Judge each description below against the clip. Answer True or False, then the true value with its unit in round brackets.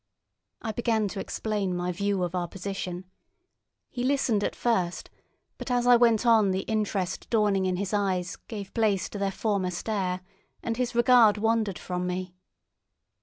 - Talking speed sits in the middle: True (165 wpm)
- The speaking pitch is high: True (205 Hz)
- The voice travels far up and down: False (3.4 semitones)